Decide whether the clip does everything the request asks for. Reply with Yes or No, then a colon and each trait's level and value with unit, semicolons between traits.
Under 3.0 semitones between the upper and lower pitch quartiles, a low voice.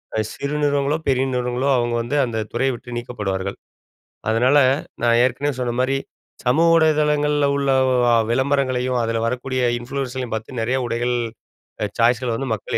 Yes: narrow, 2.6 semitones; low, 125 Hz